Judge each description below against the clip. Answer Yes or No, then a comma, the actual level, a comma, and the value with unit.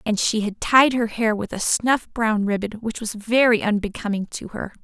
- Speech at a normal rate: No, fast, 210 wpm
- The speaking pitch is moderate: No, high, 220 Hz